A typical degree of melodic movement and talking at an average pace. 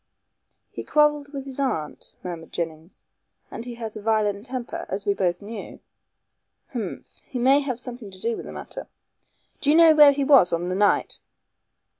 No: wide, 5.9 semitones; average, 180 wpm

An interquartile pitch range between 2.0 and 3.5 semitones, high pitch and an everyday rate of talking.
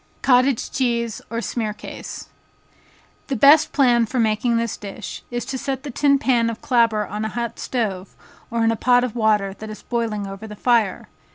Yes: narrow, 2.6 semitones; high, 235 Hz; average, 185 wpm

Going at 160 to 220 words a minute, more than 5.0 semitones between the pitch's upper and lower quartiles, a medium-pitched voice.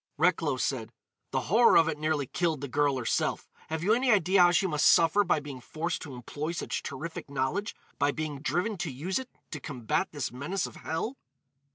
No: average, 200 wpm; average, 4.1 semitones; medium, 155 Hz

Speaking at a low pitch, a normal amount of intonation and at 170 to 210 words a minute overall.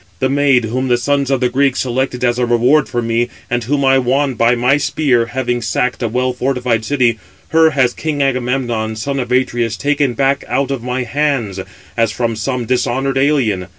No: low, 125 Hz; narrow, 2.3 semitones; average, 195 wpm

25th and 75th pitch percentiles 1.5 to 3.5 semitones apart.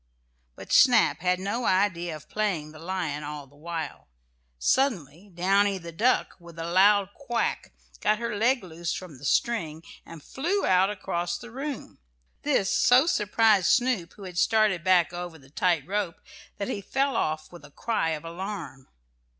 No: average, 4.4 semitones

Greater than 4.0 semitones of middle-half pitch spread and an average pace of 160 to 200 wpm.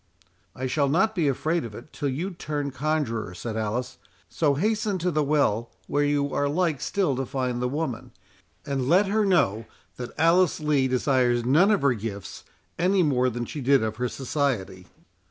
Yes: average, 4.6 semitones; average, 185 wpm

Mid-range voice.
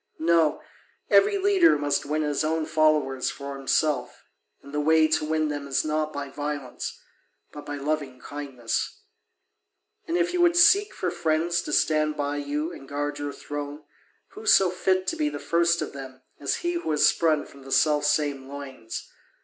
Yes: medium, 150 Hz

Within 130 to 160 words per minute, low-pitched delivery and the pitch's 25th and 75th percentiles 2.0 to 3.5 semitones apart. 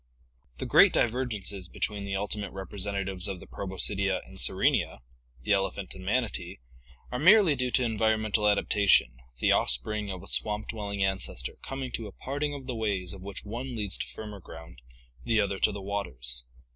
No: average, 170 wpm; low, 100 Hz; average, 2.8 semitones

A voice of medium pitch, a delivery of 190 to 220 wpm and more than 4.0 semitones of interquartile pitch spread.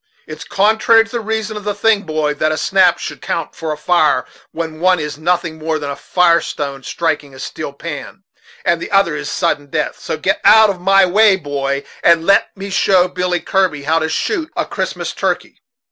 Yes: medium, 170 Hz; fast, 205 wpm; average, 4.4 semitones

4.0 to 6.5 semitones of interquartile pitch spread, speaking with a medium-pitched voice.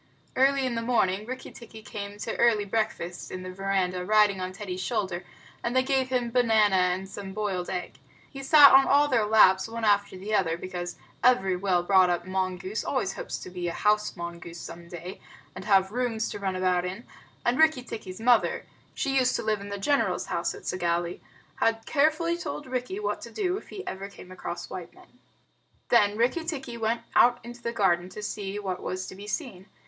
No: average, 4.6 semitones; high, 205 Hz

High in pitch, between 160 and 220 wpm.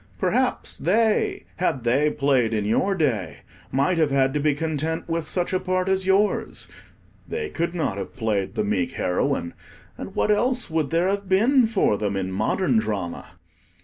No: medium, 155 Hz; average, 175 wpm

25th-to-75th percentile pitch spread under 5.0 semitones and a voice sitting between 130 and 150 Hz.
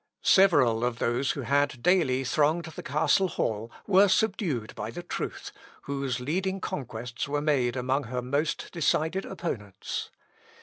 No: wide, 5.5 semitones; medium, 140 Hz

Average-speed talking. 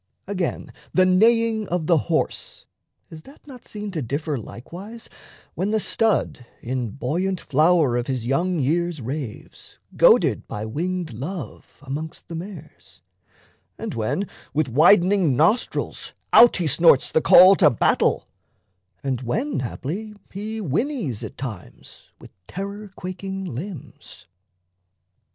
No: slow, 130 wpm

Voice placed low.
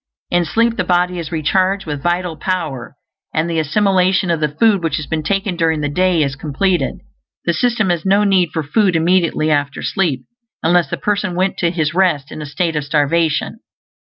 No: medium, 170 Hz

